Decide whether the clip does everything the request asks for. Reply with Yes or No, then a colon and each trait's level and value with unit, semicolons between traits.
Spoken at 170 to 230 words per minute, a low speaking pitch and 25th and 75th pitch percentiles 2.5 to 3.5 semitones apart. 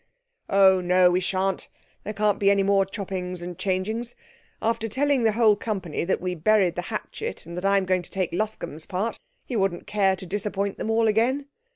No: average, 200 wpm; high, 195 Hz; average, 2.9 semitones